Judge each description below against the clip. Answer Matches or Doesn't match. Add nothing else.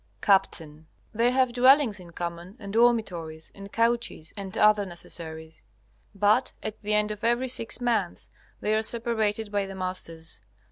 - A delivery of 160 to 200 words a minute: Doesn't match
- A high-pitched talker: Matches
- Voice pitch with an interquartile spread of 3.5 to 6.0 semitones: Matches